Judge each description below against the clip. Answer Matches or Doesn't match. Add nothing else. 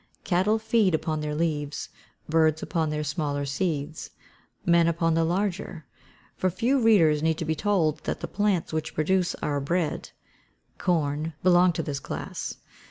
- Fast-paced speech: Doesn't match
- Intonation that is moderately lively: Matches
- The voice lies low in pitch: Doesn't match